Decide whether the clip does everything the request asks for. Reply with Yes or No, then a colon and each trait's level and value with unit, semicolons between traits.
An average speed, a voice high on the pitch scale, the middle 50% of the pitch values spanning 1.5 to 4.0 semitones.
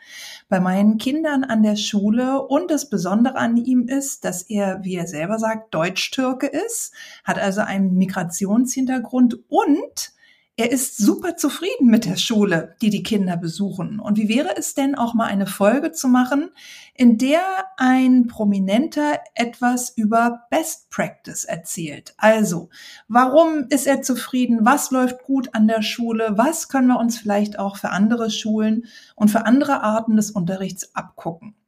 No: average, 155 wpm; high, 230 Hz; average, 4.7 semitones